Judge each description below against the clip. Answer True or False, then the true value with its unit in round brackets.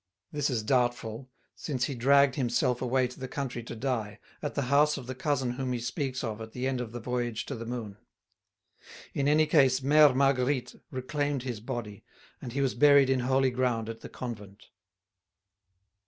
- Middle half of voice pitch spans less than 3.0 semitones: True (2.4 semitones)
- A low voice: True (125 Hz)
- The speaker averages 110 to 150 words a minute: False (185 wpm)